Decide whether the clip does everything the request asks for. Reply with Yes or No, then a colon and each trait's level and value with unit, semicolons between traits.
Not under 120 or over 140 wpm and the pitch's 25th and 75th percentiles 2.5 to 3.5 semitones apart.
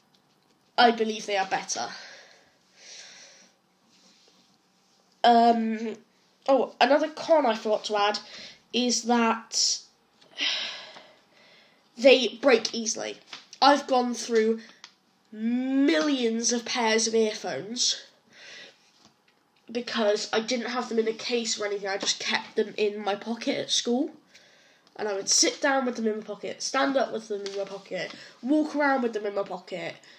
Yes: slow, 135 wpm; average, 3.0 semitones